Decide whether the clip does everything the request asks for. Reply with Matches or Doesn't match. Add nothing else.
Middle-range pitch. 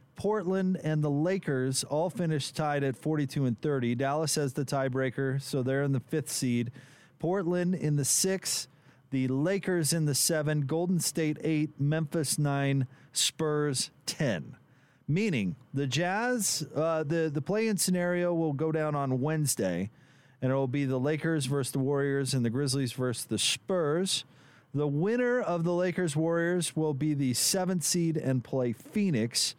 Matches